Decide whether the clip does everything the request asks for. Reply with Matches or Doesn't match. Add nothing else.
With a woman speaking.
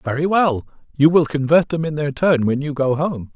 Doesn't match